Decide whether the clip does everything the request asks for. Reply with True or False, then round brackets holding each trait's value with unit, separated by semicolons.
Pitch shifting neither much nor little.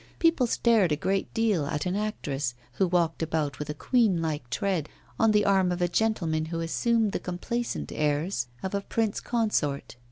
False (5.8 semitones)